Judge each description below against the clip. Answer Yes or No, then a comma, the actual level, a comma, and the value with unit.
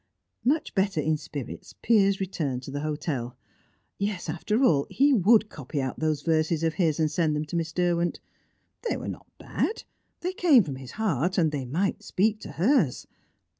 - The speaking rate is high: No, average, 180 wpm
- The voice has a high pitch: No, medium, 165 Hz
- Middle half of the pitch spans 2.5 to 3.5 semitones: No, average, 5.2 semitones